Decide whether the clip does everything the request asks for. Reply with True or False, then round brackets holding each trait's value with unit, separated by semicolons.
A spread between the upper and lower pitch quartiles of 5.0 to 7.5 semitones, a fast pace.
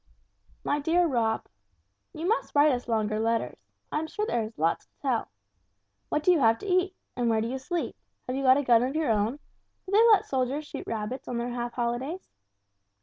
True (5.3 semitones; 215 wpm)